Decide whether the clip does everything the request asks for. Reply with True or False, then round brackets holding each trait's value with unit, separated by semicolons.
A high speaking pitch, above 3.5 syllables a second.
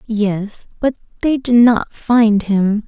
False (220 Hz; 3.0 syllables/s)